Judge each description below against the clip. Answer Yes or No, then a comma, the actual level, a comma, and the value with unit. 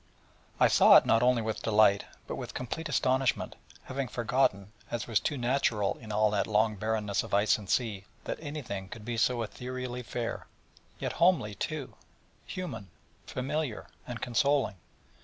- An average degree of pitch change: Yes, average, 3.5 semitones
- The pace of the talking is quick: No, average, 160 wpm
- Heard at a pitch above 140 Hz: No, low, 115 Hz